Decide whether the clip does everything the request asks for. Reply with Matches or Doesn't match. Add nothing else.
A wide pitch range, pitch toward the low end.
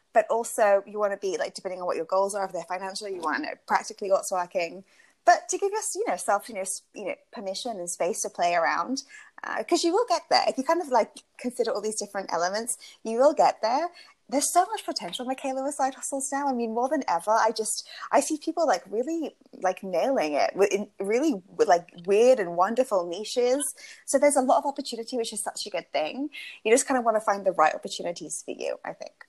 Doesn't match